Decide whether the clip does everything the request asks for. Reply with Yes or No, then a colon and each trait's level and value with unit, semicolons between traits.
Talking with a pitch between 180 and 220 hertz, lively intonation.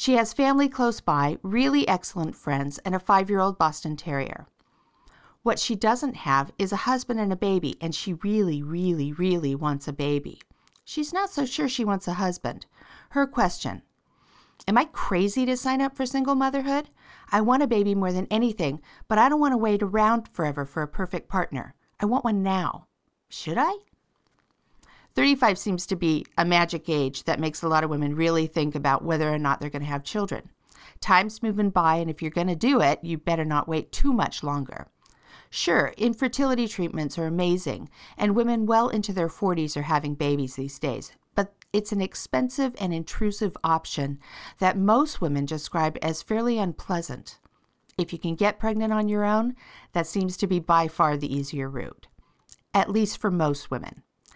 Yes: medium, 185 Hz; wide, 5.9 semitones